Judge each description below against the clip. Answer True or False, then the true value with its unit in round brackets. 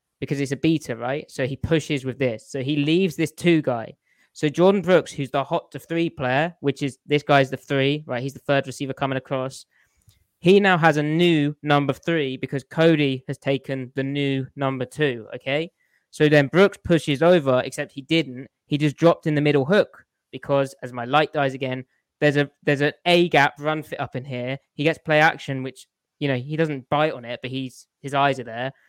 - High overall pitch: False (140 Hz)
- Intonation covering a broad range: False (2.7 semitones)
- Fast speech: True (215 wpm)